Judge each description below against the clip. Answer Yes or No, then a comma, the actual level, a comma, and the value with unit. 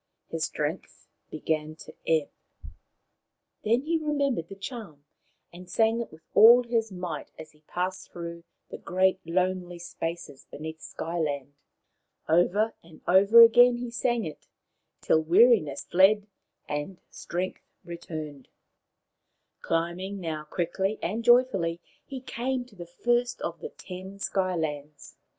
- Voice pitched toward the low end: No, medium, 180 Hz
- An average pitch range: No, wide, 5.7 semitones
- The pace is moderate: No, slow, 130 wpm